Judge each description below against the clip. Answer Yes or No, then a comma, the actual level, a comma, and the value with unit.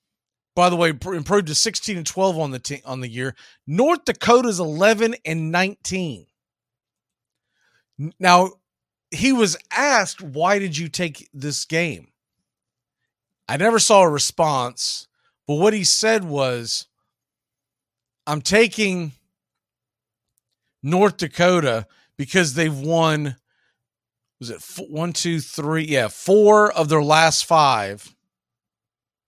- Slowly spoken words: Yes, slow, 120 wpm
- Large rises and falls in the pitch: Yes, wide, 6.5 semitones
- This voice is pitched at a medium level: Yes, medium, 160 Hz